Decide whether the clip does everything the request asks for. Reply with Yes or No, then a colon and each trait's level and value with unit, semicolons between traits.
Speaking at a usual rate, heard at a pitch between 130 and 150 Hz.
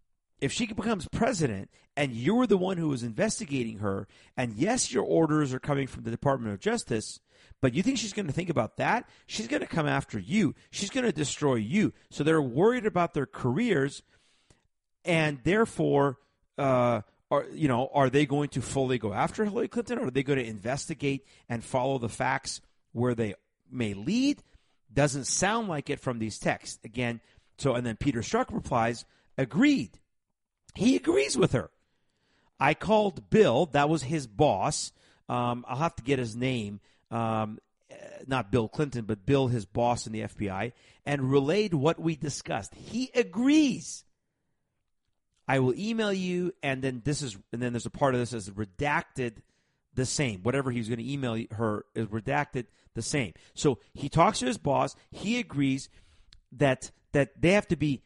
Yes: average, 175 wpm; low, 135 Hz